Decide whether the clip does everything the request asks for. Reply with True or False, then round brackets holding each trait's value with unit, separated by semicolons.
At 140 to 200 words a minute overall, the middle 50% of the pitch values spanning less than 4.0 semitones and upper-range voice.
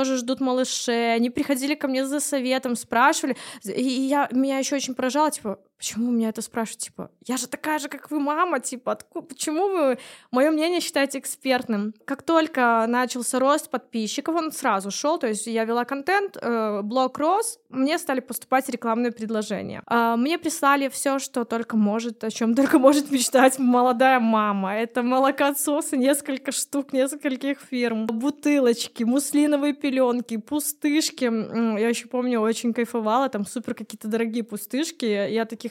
True (160 wpm; 3.4 semitones; 260 Hz)